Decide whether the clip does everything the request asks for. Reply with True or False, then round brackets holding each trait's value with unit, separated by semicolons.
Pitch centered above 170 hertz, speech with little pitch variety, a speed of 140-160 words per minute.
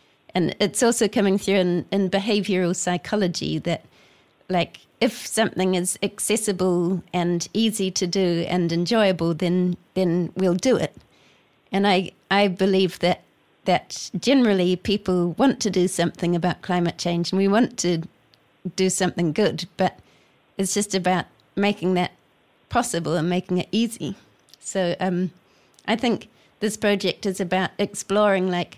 True (185 Hz; 2.3 semitones; 145 wpm)